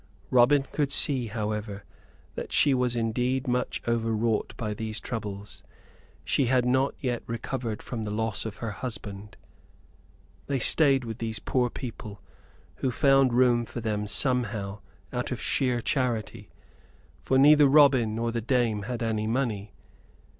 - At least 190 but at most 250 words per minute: No, average, 145 wpm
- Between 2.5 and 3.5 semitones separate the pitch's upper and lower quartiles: Yes, average, 2.9 semitones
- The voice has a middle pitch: No, low, 120 Hz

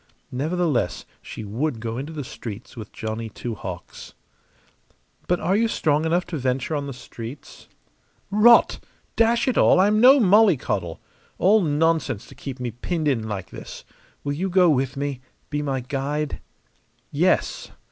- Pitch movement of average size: No, wide, 6.5 semitones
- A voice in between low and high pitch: Yes, medium, 145 Hz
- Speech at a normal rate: Yes, average, 155 wpm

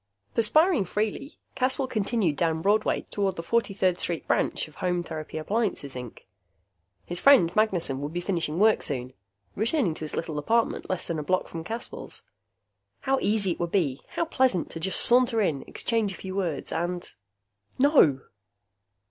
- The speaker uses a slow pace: No, average, 160 wpm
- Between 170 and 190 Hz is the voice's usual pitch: Yes, medium, 185 Hz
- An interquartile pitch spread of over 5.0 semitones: Yes, wide, 5.6 semitones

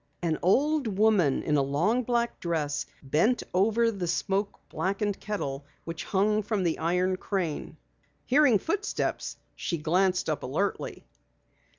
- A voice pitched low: No, high, 190 Hz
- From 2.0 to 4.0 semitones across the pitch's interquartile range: No, average, 4.7 semitones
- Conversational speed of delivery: No, slow, 130 wpm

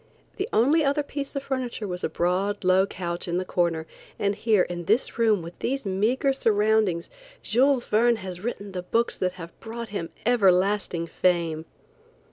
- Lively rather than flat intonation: No, average, 4.9 semitones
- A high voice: Yes, high, 205 Hz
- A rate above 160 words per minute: Yes, average, 170 wpm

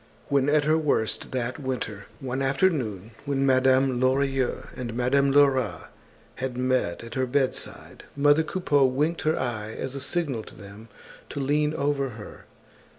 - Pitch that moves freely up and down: No, narrow, 2.5 semitones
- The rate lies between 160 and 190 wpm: No, average, 150 wpm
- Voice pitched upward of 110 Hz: Yes, low, 135 Hz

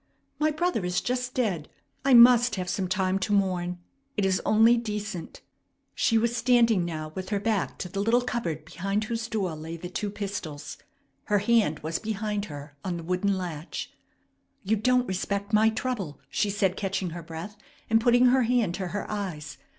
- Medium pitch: No, high, 200 Hz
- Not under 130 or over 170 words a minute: No, average, 180 wpm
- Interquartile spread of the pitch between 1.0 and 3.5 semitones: No, average, 4.1 semitones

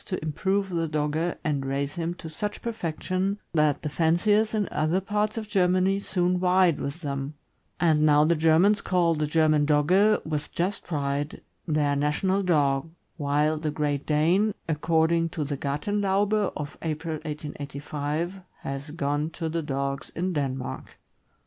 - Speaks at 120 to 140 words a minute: No, average, 150 wpm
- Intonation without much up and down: No, average, 3.8 semitones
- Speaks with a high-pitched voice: No, medium, 160 Hz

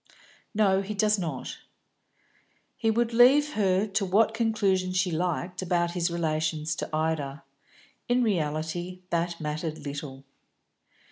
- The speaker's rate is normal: No, slow, 125 wpm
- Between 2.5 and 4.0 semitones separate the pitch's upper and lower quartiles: No, average, 4.9 semitones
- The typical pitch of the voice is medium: Yes, medium, 180 Hz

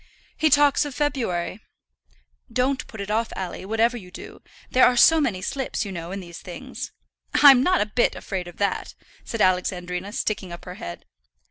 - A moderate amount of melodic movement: No, wide, 5.9 semitones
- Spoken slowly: No, average, 185 wpm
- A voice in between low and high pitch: No, high, 210 Hz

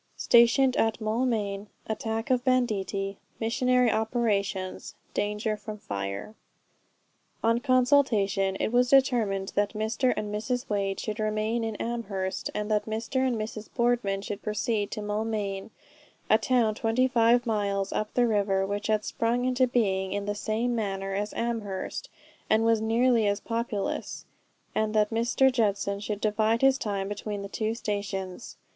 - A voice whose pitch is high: Yes, high, 215 Hz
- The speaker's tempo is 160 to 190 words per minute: No, average, 145 wpm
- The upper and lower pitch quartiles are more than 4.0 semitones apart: No, average, 2.7 semitones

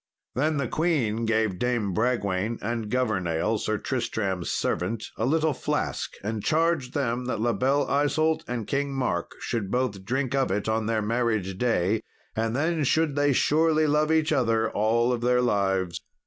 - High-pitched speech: No, low, 120 Hz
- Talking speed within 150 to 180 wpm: Yes, average, 160 wpm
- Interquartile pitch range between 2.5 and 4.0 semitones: No, average, 4.7 semitones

